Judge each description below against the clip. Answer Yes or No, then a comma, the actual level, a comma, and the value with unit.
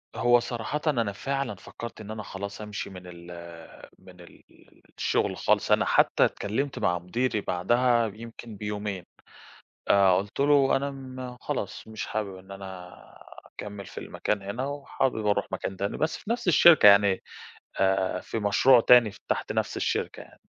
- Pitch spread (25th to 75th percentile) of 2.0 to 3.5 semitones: No, average, 4.3 semitones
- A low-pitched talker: Yes, low, 105 Hz